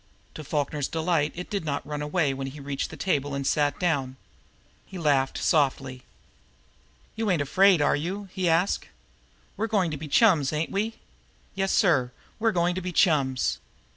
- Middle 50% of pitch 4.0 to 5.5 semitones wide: Yes, average, 4.6 semitones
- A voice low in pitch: No, medium, 155 Hz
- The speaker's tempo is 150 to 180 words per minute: Yes, average, 170 wpm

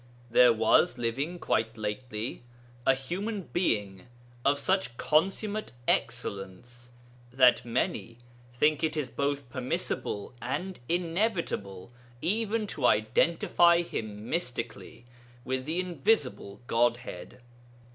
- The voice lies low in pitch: Yes, low, 130 Hz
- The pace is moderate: No, slow, 100 wpm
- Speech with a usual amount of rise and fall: No, wide, 6.8 semitones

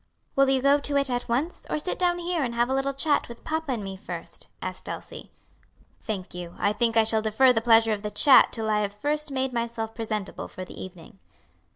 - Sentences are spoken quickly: Yes, fast, 230 wpm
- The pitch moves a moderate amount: Yes, average, 4.4 semitones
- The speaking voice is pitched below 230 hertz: No, high, 235 Hz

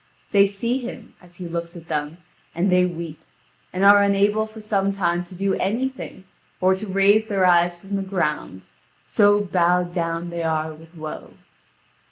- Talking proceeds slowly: No, average, 175 wpm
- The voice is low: No, medium, 185 Hz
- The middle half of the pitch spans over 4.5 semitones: No, average, 2.8 semitones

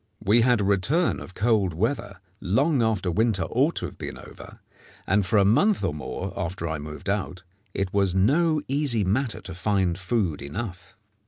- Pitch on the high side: No, low, 100 Hz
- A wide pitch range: No, average, 4.4 semitones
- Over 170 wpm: Yes, average, 180 wpm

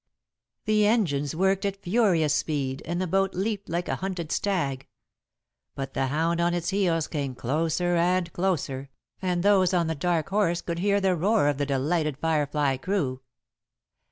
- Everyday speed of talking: Yes, average, 165 wpm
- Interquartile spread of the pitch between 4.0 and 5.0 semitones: Yes, average, 4.6 semitones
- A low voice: No, medium, 170 Hz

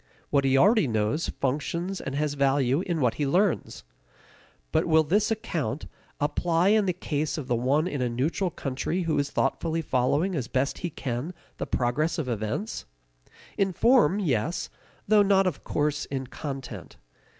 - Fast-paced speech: No, average, 165 wpm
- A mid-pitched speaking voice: Yes, medium, 150 Hz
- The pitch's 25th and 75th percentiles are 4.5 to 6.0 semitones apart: Yes, average, 5.1 semitones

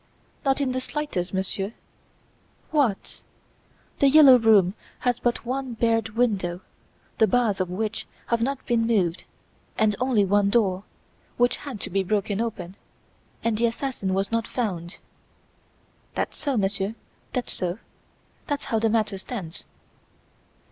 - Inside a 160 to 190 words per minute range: No, average, 140 wpm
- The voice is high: Yes, high, 225 Hz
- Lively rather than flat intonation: No, average, 4.1 semitones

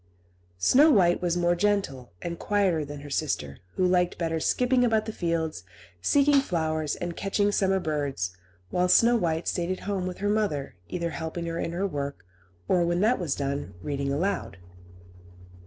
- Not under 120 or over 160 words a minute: No, average, 170 wpm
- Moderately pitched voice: Yes, medium, 175 Hz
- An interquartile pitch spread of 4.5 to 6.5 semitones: Yes, average, 4.8 semitones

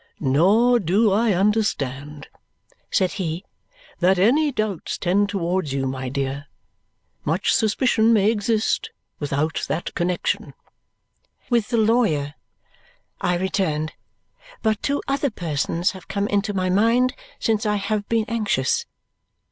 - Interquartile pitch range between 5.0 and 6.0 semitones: Yes, average, 5.3 semitones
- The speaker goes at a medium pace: No, slow, 125 wpm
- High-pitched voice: Yes, high, 200 Hz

